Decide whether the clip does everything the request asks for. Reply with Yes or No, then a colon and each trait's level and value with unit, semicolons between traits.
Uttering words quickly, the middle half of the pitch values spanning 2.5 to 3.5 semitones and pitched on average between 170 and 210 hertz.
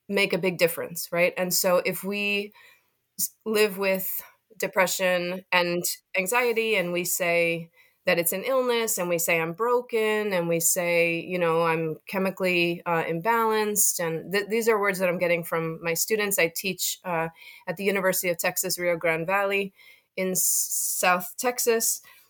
No: average, 165 wpm; average, 2.9 semitones; medium, 185 Hz